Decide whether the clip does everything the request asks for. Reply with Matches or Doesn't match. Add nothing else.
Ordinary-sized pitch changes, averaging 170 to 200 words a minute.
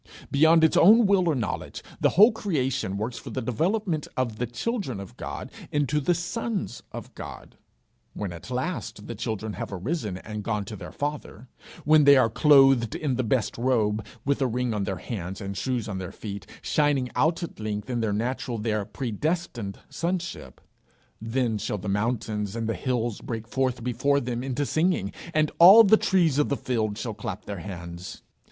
Doesn't match